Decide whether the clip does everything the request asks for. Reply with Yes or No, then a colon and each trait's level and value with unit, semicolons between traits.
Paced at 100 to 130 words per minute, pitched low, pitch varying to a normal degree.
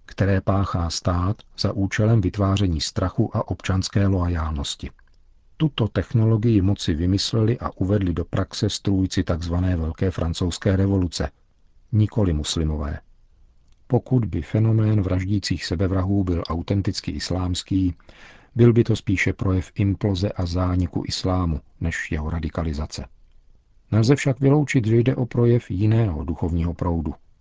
Yes: average, 120 wpm; very low, 95 Hz; average, 3.6 semitones